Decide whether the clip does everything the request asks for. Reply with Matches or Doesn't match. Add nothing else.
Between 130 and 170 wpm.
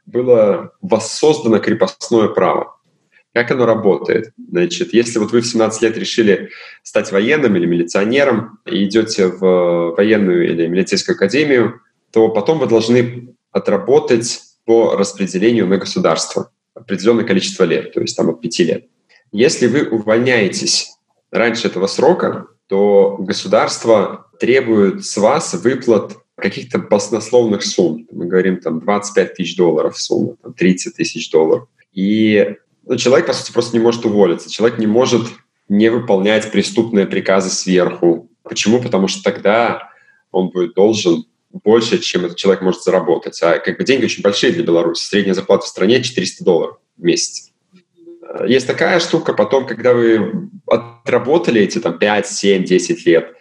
Matches